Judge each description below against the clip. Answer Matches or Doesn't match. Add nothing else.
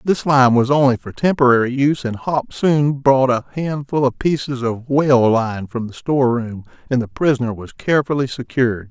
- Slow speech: Doesn't match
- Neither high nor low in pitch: Doesn't match